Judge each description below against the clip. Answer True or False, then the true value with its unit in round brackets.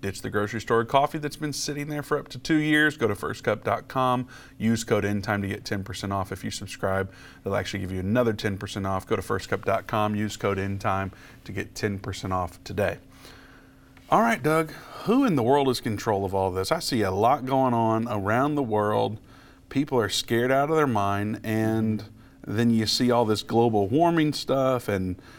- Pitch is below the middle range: True (110 Hz)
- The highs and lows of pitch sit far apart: False (4.8 semitones)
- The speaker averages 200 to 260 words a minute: True (205 wpm)